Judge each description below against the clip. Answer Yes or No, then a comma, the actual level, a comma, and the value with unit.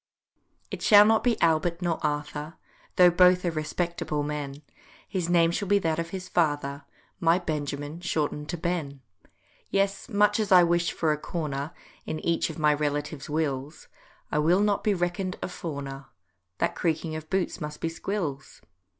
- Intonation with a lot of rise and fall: No, average, 3.3 semitones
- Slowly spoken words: No, average, 165 wpm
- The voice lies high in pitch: No, medium, 165 Hz